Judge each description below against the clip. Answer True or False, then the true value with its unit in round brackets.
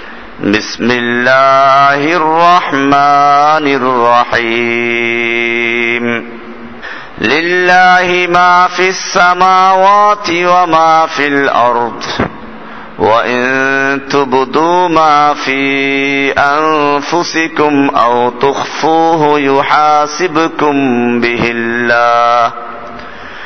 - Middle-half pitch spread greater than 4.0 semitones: True (5.2 semitones)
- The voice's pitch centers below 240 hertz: True (140 Hz)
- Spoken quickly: False (55 wpm)